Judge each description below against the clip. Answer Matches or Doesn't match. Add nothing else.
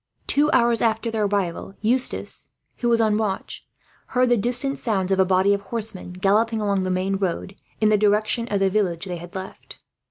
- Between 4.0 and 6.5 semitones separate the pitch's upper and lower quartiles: Doesn't match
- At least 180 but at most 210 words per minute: Matches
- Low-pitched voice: Doesn't match